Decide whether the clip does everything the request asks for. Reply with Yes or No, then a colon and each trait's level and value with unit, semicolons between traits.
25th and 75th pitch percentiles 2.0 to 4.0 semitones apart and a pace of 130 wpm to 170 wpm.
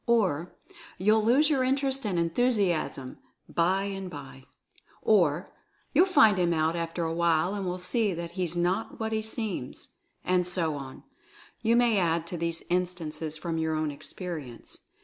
No: average, 4.7 semitones; average, 165 wpm